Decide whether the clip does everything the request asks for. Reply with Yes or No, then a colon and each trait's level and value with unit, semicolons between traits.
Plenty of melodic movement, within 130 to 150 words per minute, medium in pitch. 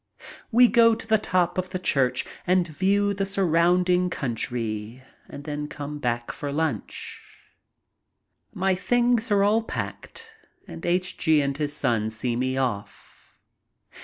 Yes: wide, 6.7 semitones; average, 140 wpm; medium, 175 Hz